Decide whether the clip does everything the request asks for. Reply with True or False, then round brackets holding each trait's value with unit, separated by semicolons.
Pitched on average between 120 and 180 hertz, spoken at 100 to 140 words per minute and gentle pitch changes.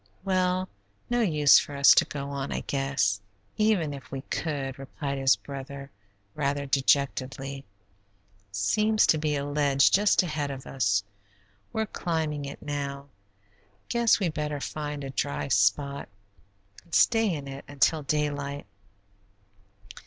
True (140 Hz; 135 wpm; 2.2 semitones)